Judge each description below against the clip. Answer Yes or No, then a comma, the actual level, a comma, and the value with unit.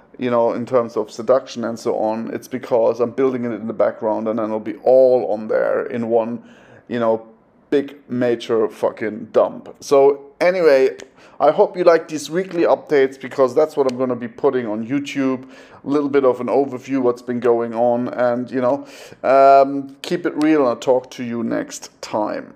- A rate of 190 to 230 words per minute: Yes, average, 200 wpm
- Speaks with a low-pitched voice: Yes, low, 130 Hz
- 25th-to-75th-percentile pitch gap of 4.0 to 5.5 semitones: No, average, 3.0 semitones